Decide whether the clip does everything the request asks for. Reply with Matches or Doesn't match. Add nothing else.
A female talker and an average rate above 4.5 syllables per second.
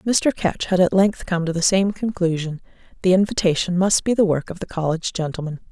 Matches